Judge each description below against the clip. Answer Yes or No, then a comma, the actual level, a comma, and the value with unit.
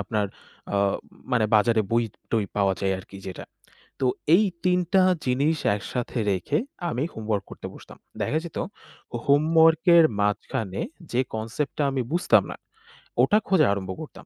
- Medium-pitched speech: No, low, 120 Hz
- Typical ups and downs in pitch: No, wide, 7.2 semitones